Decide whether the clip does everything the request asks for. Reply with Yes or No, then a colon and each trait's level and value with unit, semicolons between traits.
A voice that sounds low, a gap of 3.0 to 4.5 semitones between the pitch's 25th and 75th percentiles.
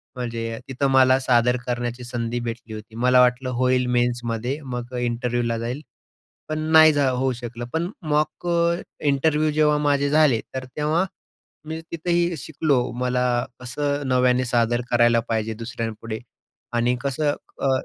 Yes: low, 125 Hz; average, 3.4 semitones